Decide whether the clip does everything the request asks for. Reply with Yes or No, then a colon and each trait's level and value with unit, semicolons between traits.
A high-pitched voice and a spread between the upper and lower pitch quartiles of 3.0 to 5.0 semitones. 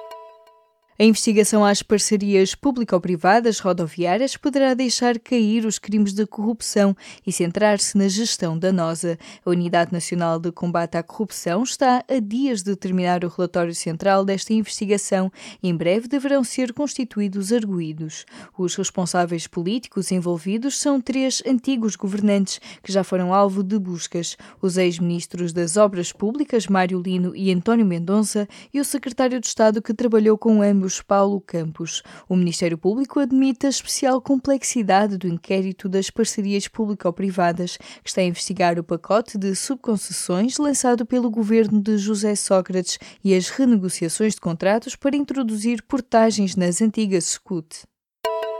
Yes: high, 200 Hz; average, 4.2 semitones